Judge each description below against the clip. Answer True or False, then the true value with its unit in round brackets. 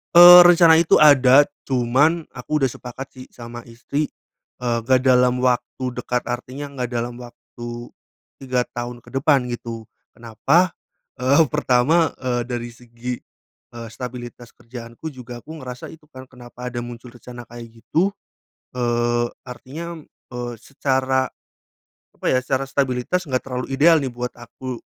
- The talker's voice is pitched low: True (125 Hz)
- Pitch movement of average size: False (2.2 semitones)